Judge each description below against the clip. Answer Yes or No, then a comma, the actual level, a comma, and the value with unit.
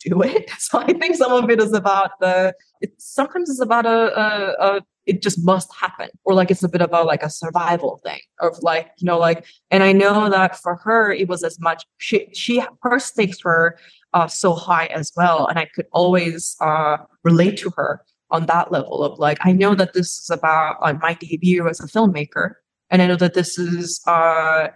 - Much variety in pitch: No, average, 3.2 semitones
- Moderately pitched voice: Yes, medium, 180 Hz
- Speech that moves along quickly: Yes, fast, 215 wpm